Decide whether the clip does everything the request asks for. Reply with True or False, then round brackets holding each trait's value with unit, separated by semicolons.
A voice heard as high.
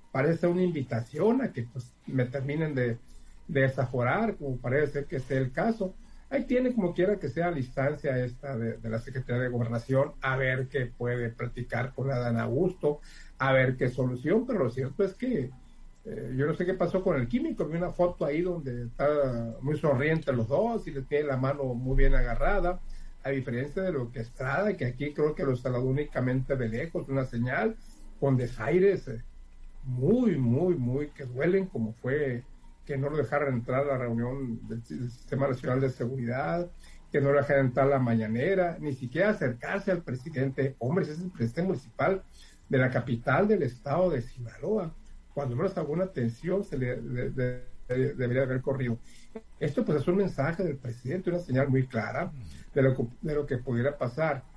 False (135 Hz)